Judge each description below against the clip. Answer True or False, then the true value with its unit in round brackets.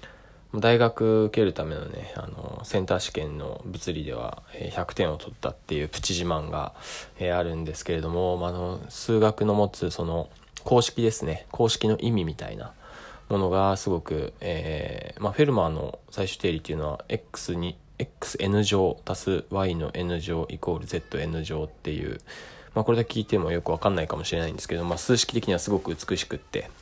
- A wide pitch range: False (4.7 semitones)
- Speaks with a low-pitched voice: True (90 Hz)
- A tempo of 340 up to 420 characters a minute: True (350 characters per minute)